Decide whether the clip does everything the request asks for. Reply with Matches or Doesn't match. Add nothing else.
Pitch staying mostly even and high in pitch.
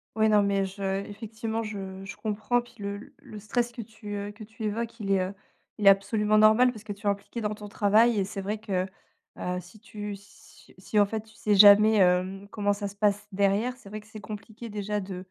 Matches